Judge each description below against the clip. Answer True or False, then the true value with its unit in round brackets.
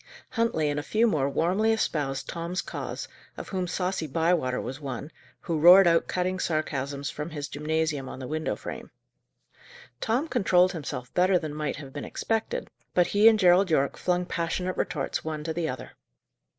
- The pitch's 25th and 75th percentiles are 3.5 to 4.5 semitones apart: True (3.9 semitones)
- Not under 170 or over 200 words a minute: True (175 wpm)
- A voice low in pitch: False (165 Hz)